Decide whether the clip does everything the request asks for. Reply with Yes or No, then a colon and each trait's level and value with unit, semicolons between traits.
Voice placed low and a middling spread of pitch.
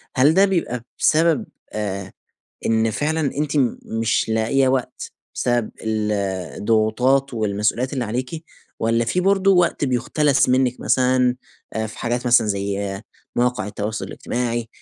Yes: low, 120 Hz; average, 3.7 semitones